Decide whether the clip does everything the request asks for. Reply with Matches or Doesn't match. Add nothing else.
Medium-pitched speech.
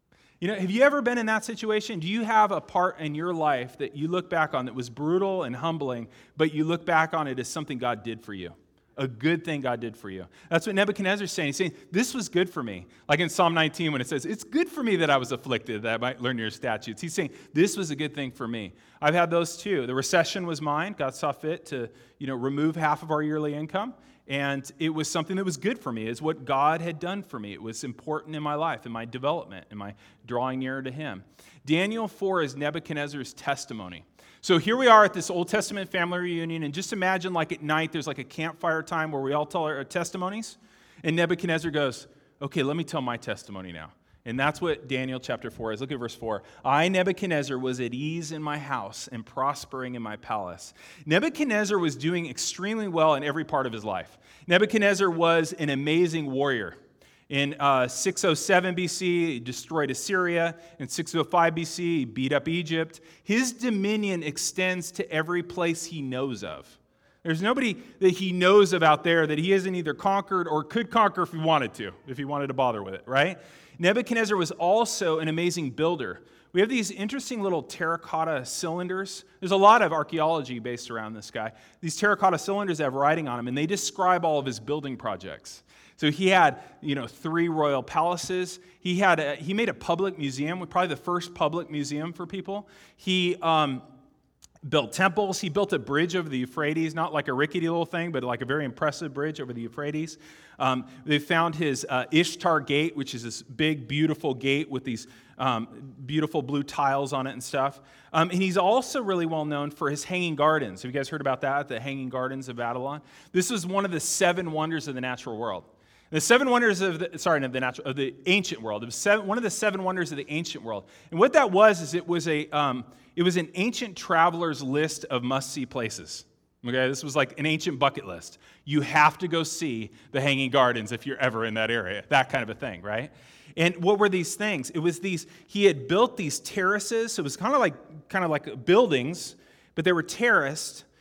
Matches